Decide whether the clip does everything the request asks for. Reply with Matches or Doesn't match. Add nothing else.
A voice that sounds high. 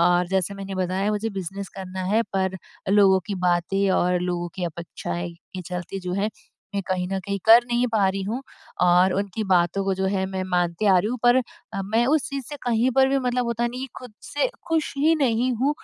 Matches